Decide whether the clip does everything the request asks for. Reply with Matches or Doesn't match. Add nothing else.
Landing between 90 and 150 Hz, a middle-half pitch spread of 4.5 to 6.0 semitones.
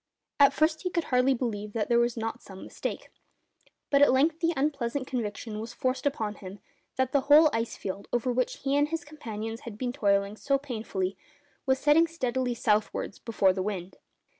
Doesn't match